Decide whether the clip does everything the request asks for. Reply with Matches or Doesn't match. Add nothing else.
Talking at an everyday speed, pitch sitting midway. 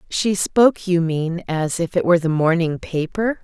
Matches